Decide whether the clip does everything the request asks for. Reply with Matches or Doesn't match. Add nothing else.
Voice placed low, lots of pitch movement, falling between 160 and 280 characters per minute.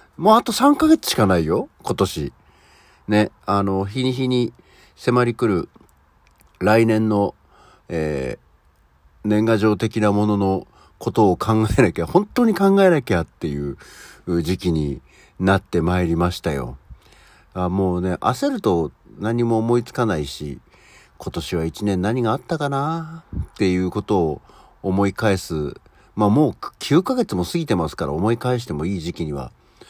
Matches